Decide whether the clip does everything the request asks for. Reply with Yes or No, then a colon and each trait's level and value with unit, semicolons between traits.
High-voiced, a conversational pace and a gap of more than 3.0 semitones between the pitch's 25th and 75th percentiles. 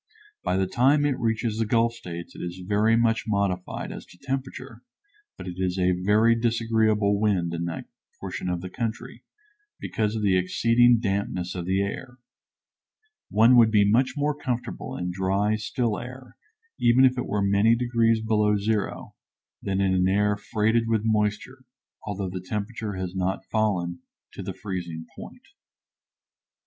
No: low, 105 Hz; average, 160 wpm; average, 3.6 semitones